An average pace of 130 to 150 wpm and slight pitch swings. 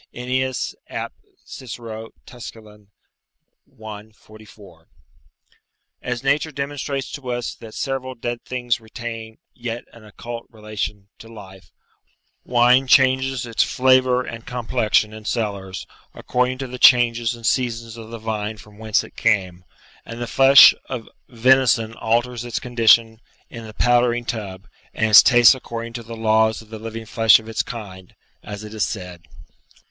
Yes: average, 145 wpm; narrow, 2.2 semitones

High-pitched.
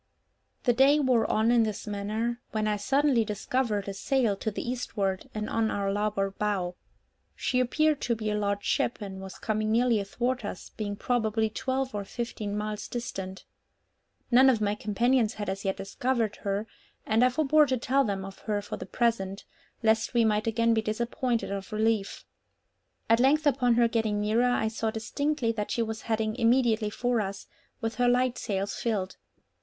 Yes: high, 220 Hz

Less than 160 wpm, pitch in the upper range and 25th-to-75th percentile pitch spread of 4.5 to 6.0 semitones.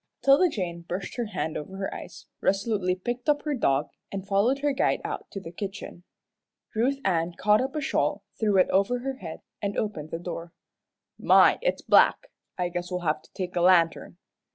No: average, 195 wpm; high, 195 Hz; wide, 5.6 semitones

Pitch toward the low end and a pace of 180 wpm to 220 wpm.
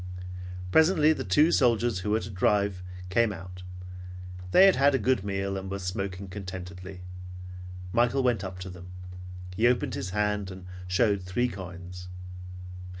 No: low, 100 Hz; average, 150 wpm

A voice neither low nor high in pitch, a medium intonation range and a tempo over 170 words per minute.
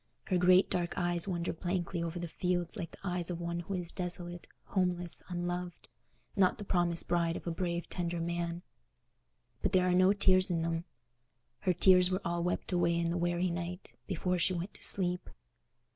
No: medium, 175 Hz; narrow, 1.1 semitones; average, 190 wpm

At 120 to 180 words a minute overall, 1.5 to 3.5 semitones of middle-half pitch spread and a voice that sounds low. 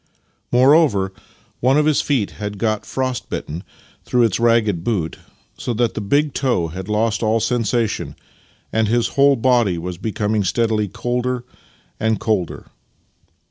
Yes: average, 145 wpm; average, 3.1 semitones; low, 115 Hz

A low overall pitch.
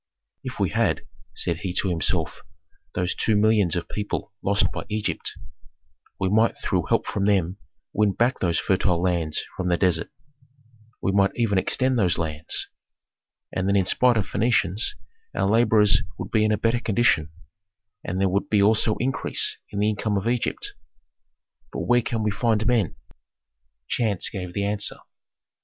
Yes: low, 100 Hz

